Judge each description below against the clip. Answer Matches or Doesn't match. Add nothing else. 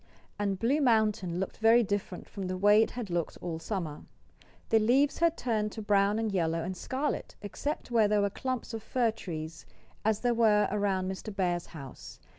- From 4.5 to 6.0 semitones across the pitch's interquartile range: Doesn't match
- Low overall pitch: Doesn't match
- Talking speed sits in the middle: Matches